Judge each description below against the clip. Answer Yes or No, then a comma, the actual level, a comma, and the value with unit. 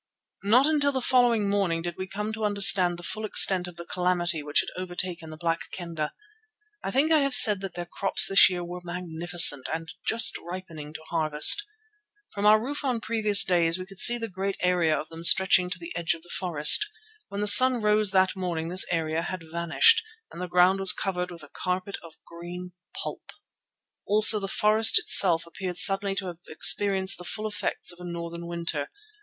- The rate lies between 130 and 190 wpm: No, average, 200 wpm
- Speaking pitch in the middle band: Yes, medium, 180 Hz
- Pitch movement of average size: Yes, average, 3.2 semitones